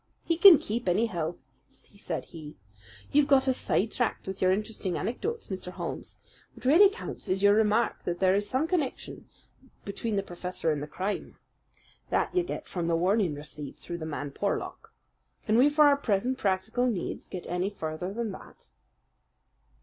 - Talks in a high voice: Yes, high, 200 Hz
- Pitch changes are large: Yes, wide, 6.0 semitones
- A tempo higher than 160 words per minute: Yes, average, 170 wpm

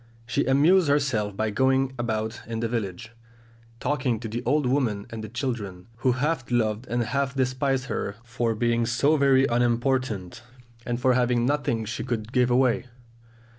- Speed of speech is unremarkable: Yes, average, 165 wpm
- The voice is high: No, low, 120 Hz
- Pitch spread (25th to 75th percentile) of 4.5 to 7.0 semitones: No, average, 2.8 semitones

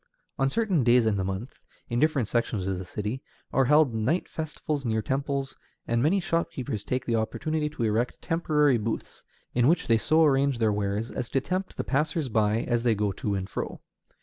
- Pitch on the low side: Yes, low, 125 Hz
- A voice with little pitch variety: No, average, 5.3 semitones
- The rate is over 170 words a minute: Yes, average, 200 wpm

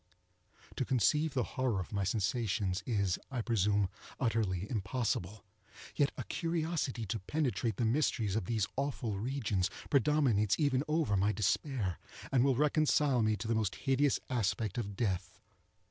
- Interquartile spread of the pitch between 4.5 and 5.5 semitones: Yes, average, 5.1 semitones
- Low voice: Yes, low, 115 Hz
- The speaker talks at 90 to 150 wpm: Yes, average, 145 wpm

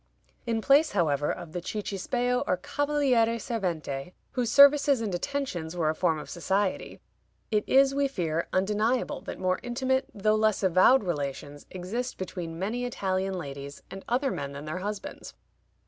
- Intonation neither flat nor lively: No, wide, 6.2 semitones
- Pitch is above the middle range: Yes, high, 195 Hz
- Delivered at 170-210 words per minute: No, average, 155 wpm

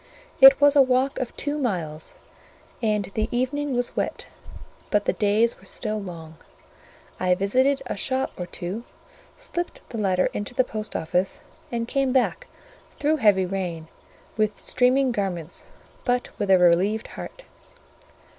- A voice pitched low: No, high, 220 Hz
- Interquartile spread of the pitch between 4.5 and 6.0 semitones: Yes, wide, 5.5 semitones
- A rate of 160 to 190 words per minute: No, average, 145 wpm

